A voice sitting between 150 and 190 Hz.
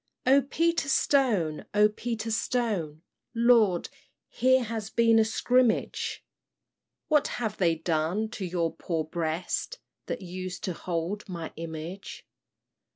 No: high, 205 Hz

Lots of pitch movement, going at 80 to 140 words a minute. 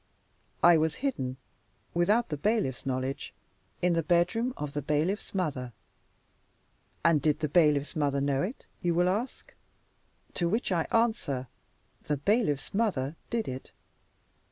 Yes: wide, 6.0 semitones; slow, 135 wpm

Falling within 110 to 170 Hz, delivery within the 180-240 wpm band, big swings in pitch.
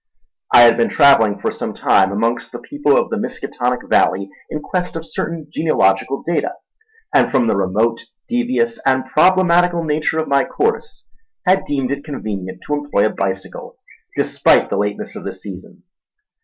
No: medium, 140 Hz; average, 165 wpm; wide, 8.2 semitones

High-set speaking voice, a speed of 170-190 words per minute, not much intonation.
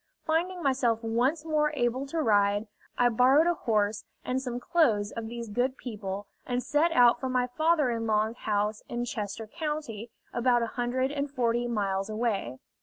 No: high, 240 Hz; average, 175 wpm; average, 3.7 semitones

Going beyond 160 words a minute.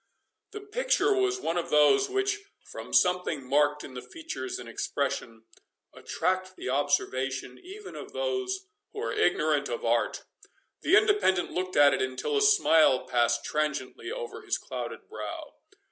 No: average, 150 wpm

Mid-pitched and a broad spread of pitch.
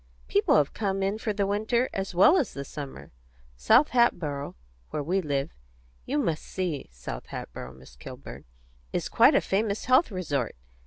Yes: medium, 180 Hz; wide, 6.6 semitones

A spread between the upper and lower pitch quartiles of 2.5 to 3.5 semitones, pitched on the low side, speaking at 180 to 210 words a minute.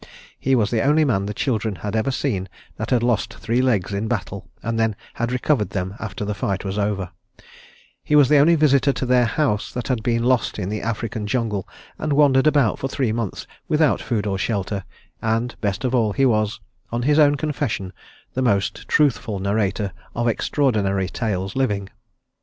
No: average, 4.3 semitones; low, 115 Hz; average, 190 wpm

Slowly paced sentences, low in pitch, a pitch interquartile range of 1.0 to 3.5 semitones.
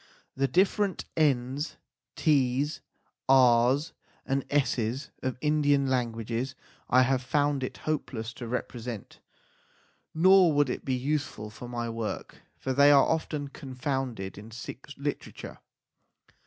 Yes: slow, 130 wpm; low, 130 Hz; average, 3.0 semitones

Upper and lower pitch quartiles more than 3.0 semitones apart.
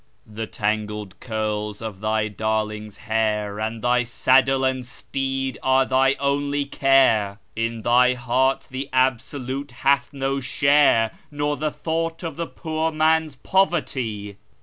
Yes: average, 4.4 semitones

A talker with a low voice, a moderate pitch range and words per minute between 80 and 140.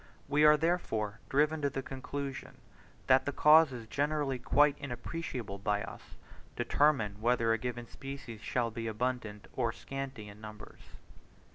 Yes: low, 130 Hz; average, 4.2 semitones; slow, 135 wpm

